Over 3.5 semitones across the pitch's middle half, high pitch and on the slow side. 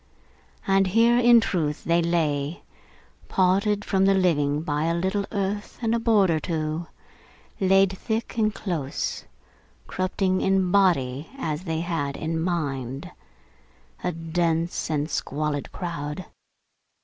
No: average, 4.0 semitones; medium, 175 Hz; slow, 125 wpm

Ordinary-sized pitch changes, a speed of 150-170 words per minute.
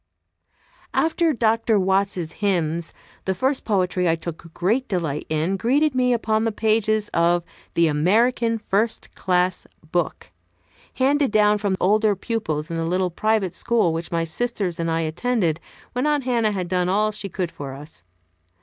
Yes: average, 5.0 semitones; average, 160 wpm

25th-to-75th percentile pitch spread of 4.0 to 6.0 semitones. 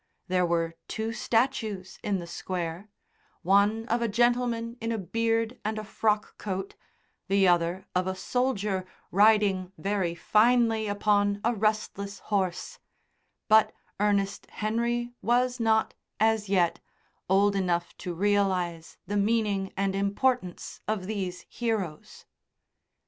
No: average, 3.0 semitones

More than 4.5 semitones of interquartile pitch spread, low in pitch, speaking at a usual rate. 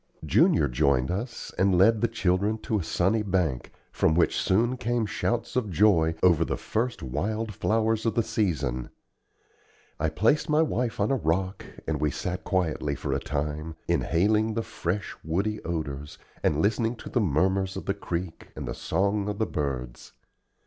Yes: wide, 5.5 semitones; very low, 95 Hz; average, 170 wpm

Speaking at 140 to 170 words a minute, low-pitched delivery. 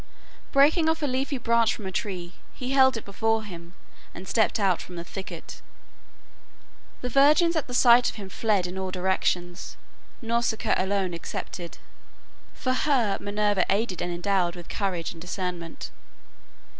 No: average, 150 wpm; high, 205 Hz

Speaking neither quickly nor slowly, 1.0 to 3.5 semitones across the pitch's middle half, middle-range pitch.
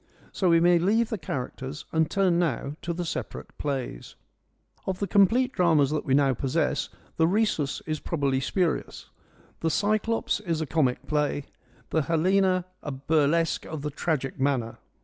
No: average, 165 wpm; average, 4.4 semitones; medium, 160 Hz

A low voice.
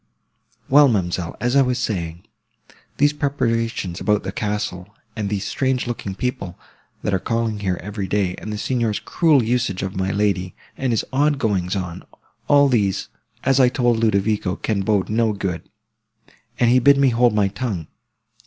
Yes: low, 110 Hz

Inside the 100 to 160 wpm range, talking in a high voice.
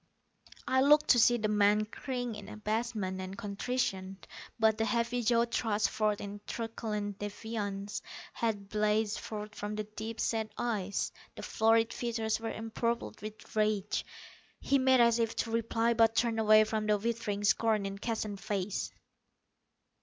Yes: average, 155 wpm; high, 220 Hz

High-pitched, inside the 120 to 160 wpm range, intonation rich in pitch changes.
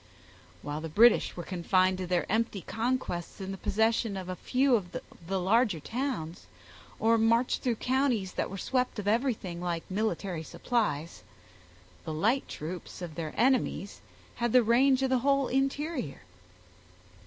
Yes: high, 215 Hz; average, 155 wpm; wide, 5.8 semitones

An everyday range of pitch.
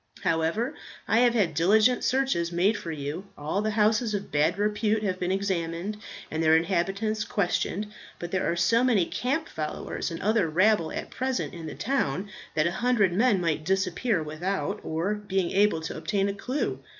Yes: average, 4.4 semitones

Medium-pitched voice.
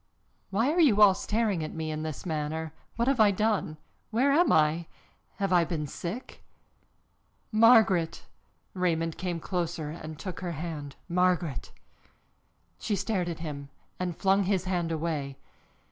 Yes: medium, 175 Hz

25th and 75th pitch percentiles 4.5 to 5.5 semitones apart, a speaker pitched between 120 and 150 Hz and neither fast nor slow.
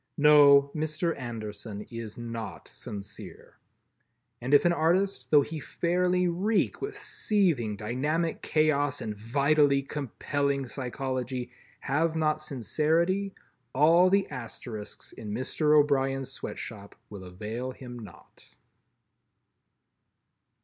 No: average, 5.1 semitones; medium, 140 Hz; slow, 105 wpm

